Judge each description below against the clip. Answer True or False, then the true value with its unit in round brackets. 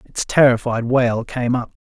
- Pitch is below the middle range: True (120 Hz)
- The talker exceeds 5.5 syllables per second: False (4.3 syllables/s)